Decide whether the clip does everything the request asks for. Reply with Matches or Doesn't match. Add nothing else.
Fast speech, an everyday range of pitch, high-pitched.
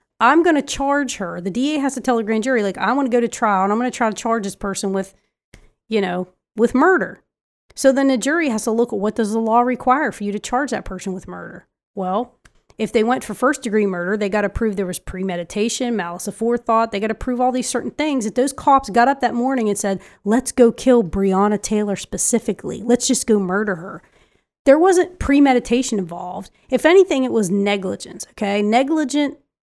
Matches